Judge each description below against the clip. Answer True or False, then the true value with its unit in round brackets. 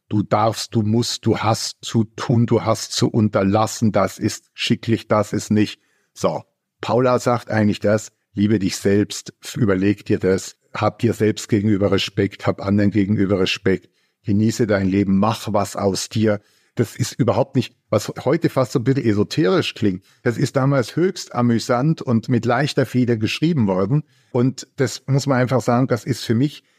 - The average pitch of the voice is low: True (110 Hz)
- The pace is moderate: True (175 wpm)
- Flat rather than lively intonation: False (3.5 semitones)